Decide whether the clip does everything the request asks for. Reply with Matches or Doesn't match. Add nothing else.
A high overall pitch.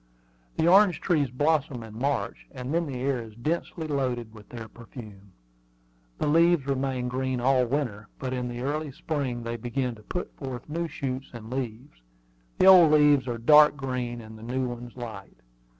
Doesn't match